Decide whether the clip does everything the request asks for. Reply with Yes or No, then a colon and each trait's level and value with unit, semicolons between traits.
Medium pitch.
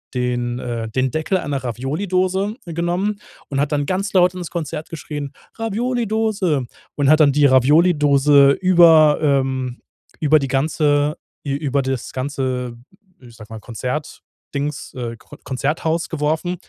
Yes: medium, 145 Hz